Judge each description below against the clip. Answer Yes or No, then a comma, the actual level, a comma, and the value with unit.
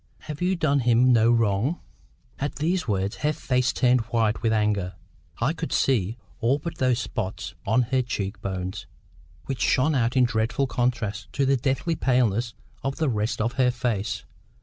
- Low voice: Yes, low, 120 Hz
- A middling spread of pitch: Yes, average, 3.5 semitones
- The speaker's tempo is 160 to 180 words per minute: Yes, average, 165 wpm